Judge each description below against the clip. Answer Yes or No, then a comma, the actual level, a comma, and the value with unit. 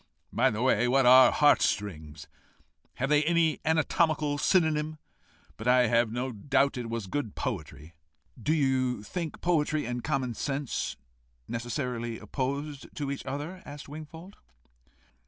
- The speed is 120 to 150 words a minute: Yes, average, 140 wpm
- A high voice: No, low, 135 Hz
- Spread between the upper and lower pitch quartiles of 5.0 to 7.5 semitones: No, average, 4.1 semitones